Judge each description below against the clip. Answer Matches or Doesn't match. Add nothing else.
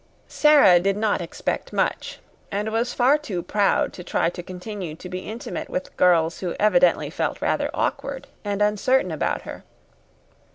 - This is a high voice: Matches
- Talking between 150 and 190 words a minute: Matches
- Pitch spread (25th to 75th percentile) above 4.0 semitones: Doesn't match